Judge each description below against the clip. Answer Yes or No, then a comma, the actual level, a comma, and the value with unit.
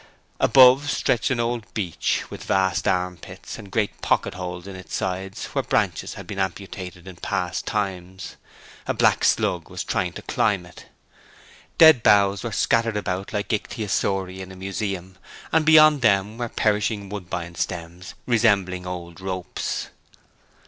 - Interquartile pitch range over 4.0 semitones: No, average, 3.0 semitones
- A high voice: No, very low, 95 Hz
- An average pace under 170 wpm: Yes, average, 150 wpm